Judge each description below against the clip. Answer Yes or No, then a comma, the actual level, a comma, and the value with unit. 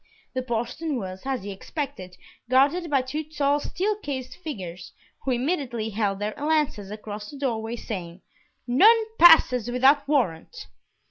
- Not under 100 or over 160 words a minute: Yes, average, 145 wpm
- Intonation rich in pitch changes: Yes, wide, 5.7 semitones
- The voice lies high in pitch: Yes, very high, 255 Hz